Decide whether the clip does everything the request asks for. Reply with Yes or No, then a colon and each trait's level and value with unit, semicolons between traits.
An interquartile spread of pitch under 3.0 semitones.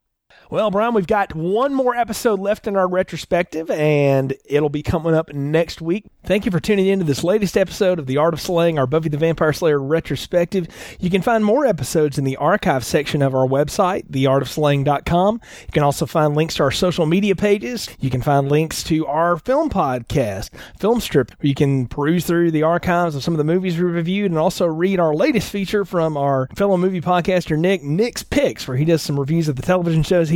No: average, 4.3 semitones